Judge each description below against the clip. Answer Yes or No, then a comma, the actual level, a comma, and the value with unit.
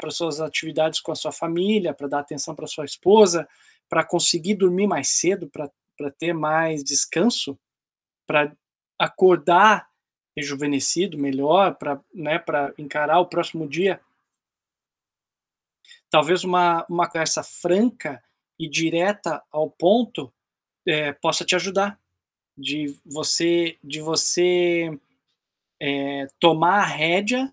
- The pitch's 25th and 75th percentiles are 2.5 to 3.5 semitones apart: Yes, average, 3.1 semitones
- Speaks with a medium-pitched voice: Yes, medium, 165 Hz